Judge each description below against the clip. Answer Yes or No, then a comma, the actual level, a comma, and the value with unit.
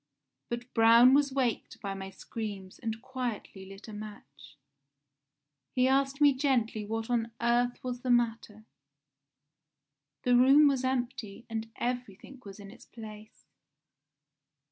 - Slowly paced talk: Yes, slow, 130 wpm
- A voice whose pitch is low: No, high, 235 Hz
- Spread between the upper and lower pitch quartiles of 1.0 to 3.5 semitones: Yes, average, 3.1 semitones